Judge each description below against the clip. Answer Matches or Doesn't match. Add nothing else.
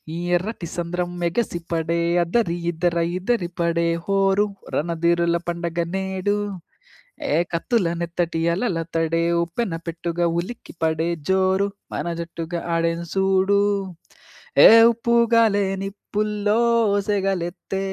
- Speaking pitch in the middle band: Matches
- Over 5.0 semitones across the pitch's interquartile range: Doesn't match